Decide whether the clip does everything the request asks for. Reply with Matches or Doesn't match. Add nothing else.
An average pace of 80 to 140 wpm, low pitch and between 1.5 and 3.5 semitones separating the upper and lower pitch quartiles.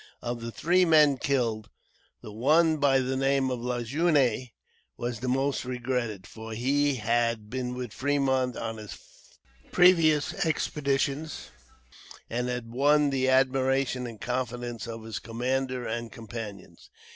Matches